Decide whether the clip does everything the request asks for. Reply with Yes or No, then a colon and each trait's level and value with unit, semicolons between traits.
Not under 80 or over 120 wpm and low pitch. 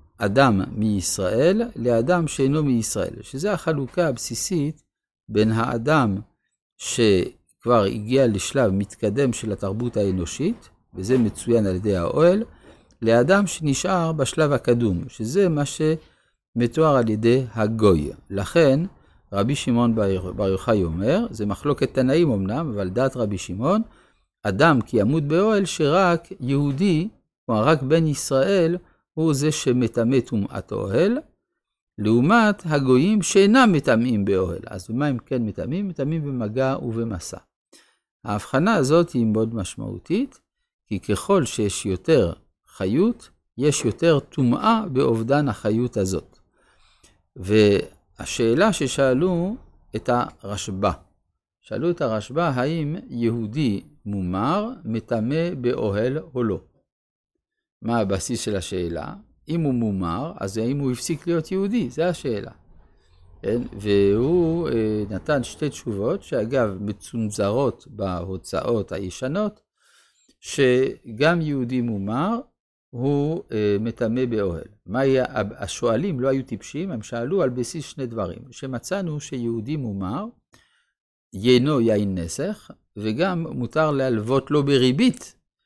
Yes: average, 110 wpm; low, 120 Hz